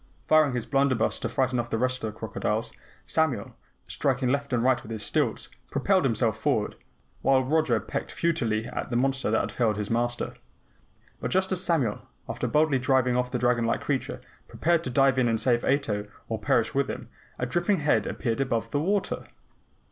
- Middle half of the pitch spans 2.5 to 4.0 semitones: Yes, average, 3.4 semitones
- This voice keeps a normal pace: Yes, average, 195 wpm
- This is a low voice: Yes, low, 130 Hz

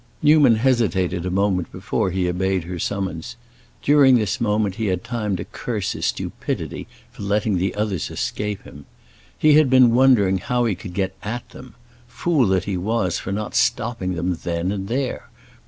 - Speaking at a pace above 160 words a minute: Yes, average, 175 wpm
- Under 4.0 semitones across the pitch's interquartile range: No, average, 4.4 semitones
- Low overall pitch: Yes, low, 100 Hz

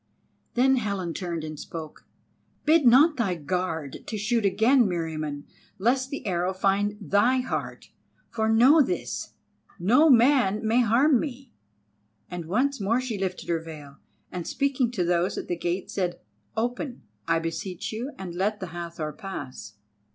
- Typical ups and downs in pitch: No, wide, 6.1 semitones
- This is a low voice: No, high, 200 Hz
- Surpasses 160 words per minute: No, average, 150 wpm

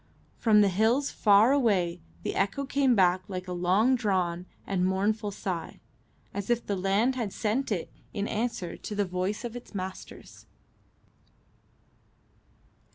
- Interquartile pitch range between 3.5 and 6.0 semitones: Yes, average, 3.8 semitones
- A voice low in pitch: No, high, 205 Hz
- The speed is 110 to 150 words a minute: Yes, average, 145 wpm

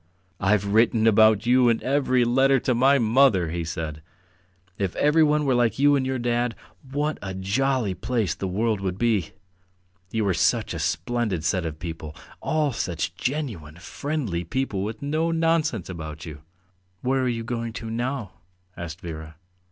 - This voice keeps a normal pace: Yes, average, 165 wpm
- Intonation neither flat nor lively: No, wide, 6.1 semitones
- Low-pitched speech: Yes, low, 115 Hz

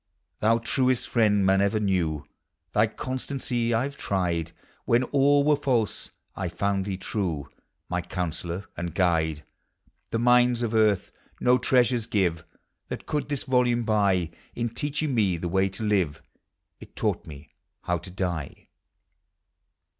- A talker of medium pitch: No, low, 105 Hz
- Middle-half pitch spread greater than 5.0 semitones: Yes, wide, 5.5 semitones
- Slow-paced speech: No, average, 145 wpm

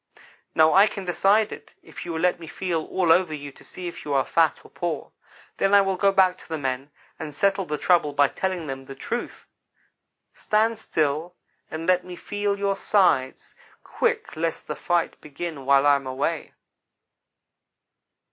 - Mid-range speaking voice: Yes, medium, 170 Hz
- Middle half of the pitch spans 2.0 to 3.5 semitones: No, average, 4.6 semitones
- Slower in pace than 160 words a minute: No, average, 185 wpm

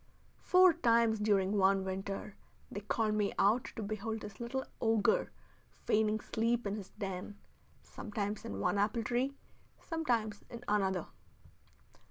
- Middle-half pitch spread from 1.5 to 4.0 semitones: Yes, narrow, 2.6 semitones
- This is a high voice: Yes, high, 215 Hz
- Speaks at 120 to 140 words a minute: Yes, slow, 135 wpm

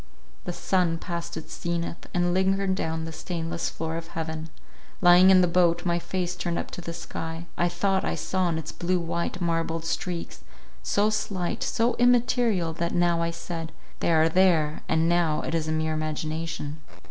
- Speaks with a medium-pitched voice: Yes, medium, 170 Hz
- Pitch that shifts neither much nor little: No, narrow, 1.8 semitones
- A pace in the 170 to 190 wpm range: Yes, average, 180 wpm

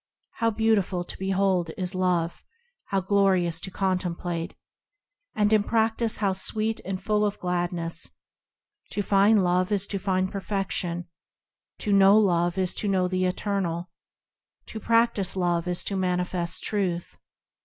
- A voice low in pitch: No, high, 190 Hz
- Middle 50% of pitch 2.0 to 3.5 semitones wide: Yes, narrow, 2.4 semitones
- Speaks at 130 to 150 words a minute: Yes, average, 140 wpm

